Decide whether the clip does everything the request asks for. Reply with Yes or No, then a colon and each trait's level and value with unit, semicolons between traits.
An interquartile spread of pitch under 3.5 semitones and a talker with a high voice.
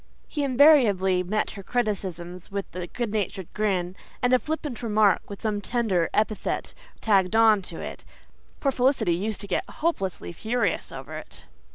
No: average, 4.5 semitones; high, 210 Hz